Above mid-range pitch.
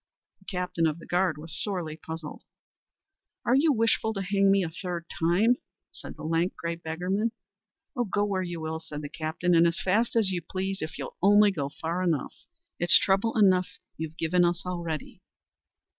No: medium, 180 Hz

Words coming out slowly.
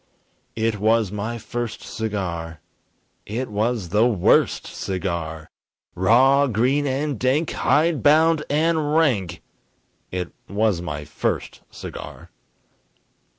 Yes: slow, 105 wpm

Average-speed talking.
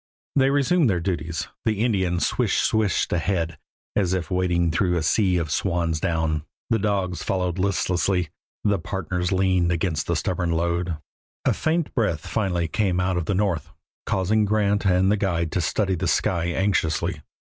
Yes: average, 165 wpm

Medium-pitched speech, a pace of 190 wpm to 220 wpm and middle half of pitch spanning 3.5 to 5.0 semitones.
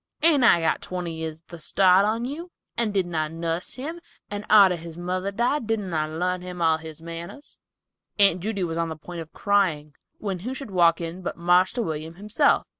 Yes: medium, 180 Hz; average, 200 wpm; average, 4.0 semitones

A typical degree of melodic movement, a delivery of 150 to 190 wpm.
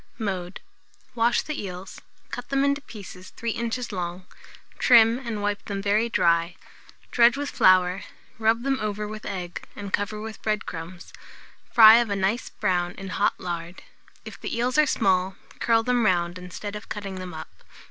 Yes: average, 4.1 semitones; average, 170 wpm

